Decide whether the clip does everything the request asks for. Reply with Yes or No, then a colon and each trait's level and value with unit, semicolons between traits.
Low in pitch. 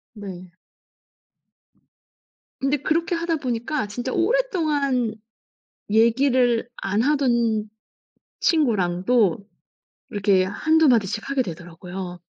No: high, 235 Hz